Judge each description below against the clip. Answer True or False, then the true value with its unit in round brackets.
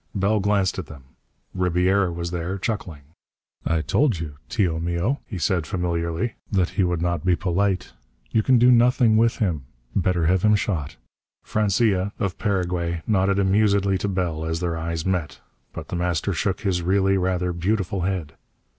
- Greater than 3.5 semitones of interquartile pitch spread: False (2.8 semitones)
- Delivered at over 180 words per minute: False (165 wpm)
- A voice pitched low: True (90 Hz)